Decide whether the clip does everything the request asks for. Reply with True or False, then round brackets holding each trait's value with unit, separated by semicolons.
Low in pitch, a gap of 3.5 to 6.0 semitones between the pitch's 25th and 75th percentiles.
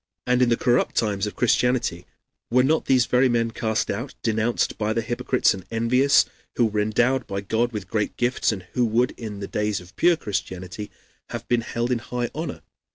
False (115 Hz; 2.8 semitones)